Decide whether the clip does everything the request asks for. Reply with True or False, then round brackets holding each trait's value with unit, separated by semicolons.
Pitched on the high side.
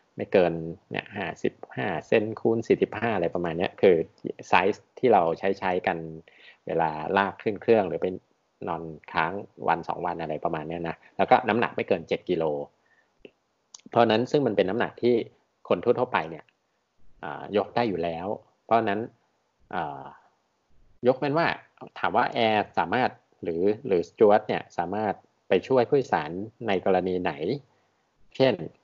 False (90 Hz)